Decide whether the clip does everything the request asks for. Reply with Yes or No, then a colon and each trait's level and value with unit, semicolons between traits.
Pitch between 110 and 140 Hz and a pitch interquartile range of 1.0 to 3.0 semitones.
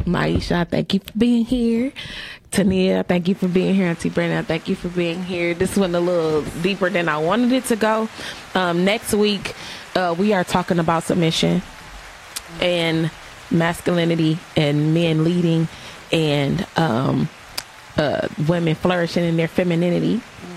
No: medium, 175 Hz; average, 2.7 semitones